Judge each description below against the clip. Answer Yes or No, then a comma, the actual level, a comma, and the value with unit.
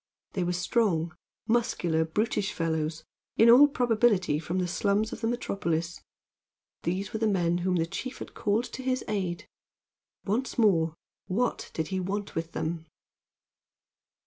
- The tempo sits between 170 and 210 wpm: No, average, 145 wpm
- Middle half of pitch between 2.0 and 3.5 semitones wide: No, average, 5.0 semitones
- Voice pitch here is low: No, high, 190 Hz